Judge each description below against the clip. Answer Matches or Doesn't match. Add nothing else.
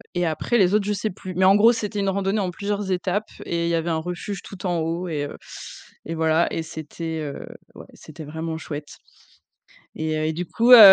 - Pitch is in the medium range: Matches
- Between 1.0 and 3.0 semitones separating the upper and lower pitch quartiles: Doesn't match